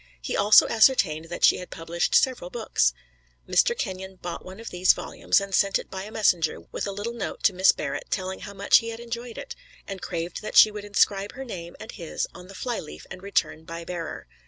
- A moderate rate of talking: No, fast, 225 wpm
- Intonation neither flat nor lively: Yes, average, 3.8 semitones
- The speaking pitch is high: Yes, high, 195 Hz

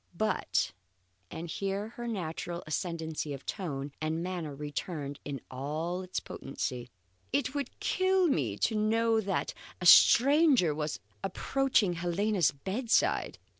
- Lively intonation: Yes, wide, 6.5 semitones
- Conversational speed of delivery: No, slow, 125 wpm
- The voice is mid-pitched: Yes, medium, 175 Hz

